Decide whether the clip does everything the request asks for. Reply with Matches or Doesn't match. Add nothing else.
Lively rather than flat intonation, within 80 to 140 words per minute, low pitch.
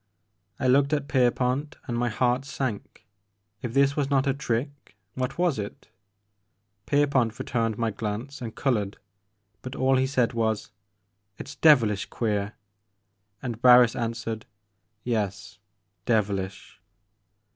Doesn't match